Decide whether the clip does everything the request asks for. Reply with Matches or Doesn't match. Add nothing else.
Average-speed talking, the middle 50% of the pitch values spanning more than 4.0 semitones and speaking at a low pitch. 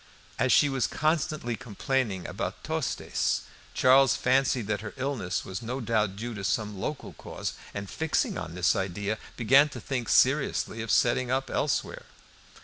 Matches